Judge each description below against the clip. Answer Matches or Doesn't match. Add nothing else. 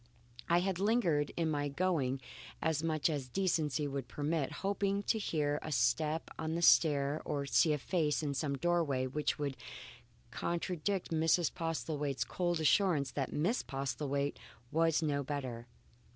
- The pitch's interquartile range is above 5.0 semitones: Doesn't match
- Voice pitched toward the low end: Doesn't match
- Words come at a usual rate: Matches